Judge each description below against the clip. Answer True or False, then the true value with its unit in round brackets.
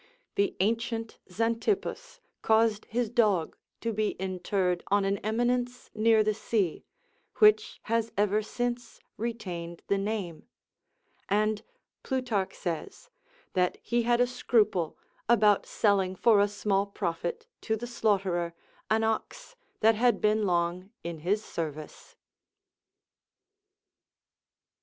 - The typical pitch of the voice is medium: False (215 Hz)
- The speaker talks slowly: True (115 wpm)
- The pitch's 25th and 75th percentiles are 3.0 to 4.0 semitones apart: True (3.4 semitones)